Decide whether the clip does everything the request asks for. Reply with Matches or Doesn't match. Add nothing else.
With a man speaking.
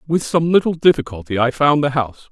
Matches